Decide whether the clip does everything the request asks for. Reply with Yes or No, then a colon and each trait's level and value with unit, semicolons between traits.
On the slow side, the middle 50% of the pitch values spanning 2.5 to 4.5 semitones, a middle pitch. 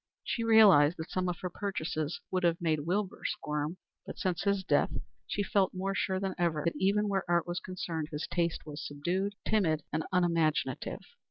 No: average, 185 wpm; average, 3.3 semitones; medium, 175 Hz